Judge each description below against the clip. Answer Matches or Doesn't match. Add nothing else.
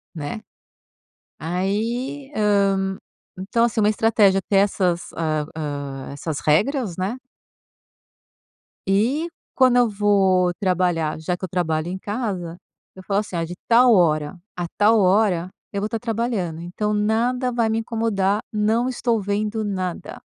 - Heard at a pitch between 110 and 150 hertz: Doesn't match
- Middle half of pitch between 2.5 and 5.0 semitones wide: Matches